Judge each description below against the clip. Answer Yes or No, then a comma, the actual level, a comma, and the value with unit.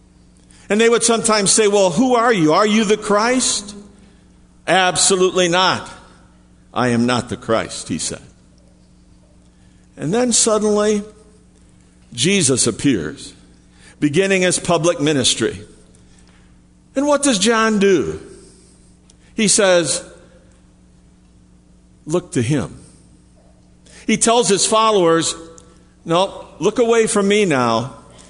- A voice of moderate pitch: Yes, medium, 155 Hz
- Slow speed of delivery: Yes, slow, 110 wpm